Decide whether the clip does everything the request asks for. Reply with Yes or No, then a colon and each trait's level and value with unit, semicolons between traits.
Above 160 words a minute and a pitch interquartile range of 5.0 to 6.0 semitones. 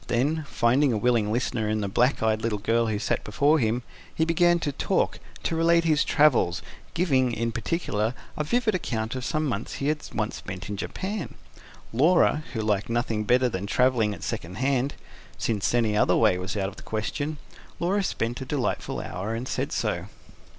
Yes: average, 190 wpm; wide, 5.6 semitones